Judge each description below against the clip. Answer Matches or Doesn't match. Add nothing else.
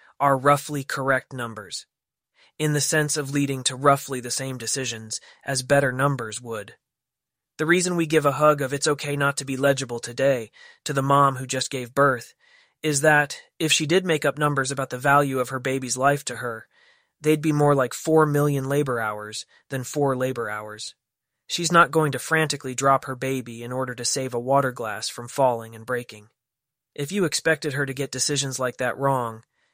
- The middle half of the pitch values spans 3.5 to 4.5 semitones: Doesn't match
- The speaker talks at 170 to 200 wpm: Matches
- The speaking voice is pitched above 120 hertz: Matches